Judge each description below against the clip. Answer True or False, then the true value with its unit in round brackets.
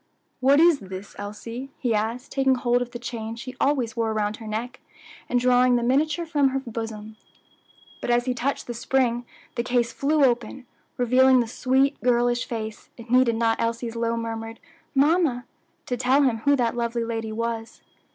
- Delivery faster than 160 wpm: True (180 wpm)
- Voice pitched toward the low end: False (240 Hz)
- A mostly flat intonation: True (2.2 semitones)